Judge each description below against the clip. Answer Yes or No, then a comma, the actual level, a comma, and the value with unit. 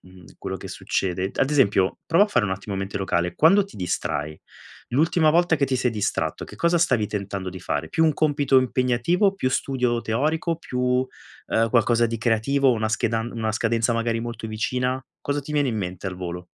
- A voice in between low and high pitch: No, low, 120 Hz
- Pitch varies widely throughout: Yes, wide, 5.8 semitones